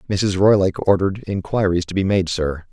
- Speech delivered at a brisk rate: No, average, 175 wpm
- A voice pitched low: Yes, very low, 95 Hz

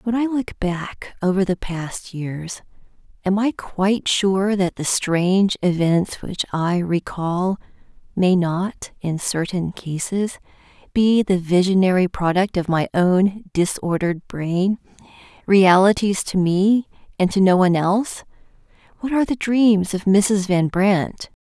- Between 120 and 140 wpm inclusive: Yes, slow, 135 wpm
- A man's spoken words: No, female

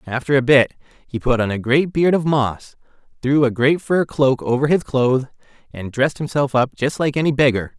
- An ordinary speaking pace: No, fast, 210 wpm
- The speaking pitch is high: No, low, 135 Hz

